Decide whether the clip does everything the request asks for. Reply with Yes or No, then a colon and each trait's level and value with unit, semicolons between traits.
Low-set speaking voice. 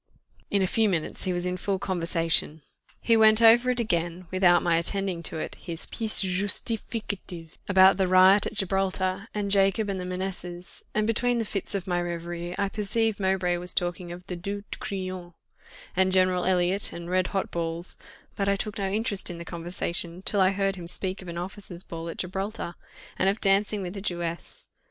No: medium, 185 Hz